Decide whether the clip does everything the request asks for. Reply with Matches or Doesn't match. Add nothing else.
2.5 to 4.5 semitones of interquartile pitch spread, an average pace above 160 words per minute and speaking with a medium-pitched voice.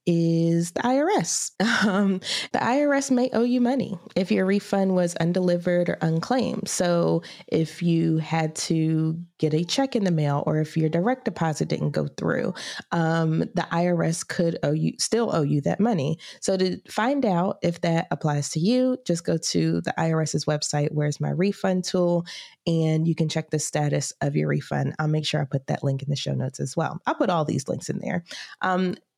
Matches